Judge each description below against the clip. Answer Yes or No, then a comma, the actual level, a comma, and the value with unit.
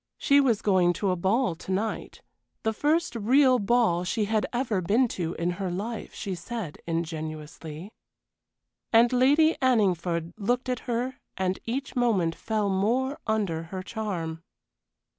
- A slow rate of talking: No, average, 145 wpm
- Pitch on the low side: No, high, 210 Hz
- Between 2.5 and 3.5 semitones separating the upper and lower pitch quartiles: No, wide, 5.6 semitones